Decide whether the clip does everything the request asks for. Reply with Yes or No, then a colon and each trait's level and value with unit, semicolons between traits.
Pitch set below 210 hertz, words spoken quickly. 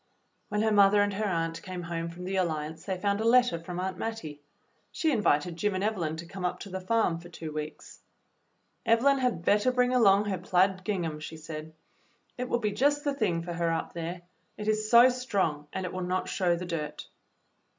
Yes: medium, 185 Hz; fast, 215 wpm